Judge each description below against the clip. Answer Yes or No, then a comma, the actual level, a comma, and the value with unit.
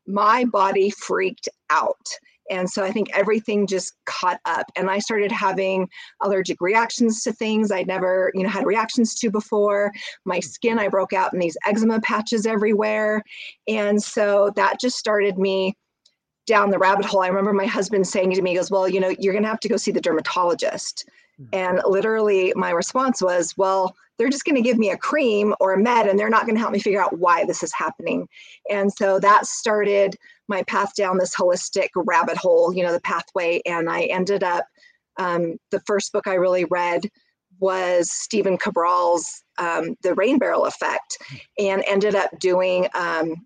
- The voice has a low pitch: No, high, 200 Hz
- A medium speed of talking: Yes, average, 190 wpm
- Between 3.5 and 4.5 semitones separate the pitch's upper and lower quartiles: No, narrow, 2.5 semitones